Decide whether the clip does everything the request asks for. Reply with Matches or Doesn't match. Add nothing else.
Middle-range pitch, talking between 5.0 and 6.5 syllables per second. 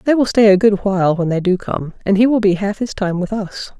Doesn't match